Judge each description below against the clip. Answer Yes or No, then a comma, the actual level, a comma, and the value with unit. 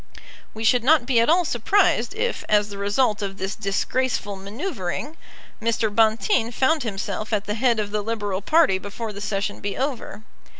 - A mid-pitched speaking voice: No, high, 220 Hz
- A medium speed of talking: Yes, average, 175 wpm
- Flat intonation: No, average, 4.2 semitones